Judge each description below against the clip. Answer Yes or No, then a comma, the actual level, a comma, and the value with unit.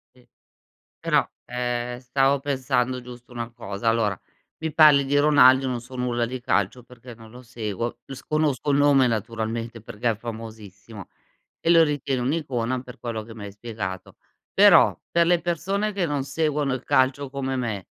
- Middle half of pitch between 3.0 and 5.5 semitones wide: Yes, average, 3.4 semitones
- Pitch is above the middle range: No, low, 125 Hz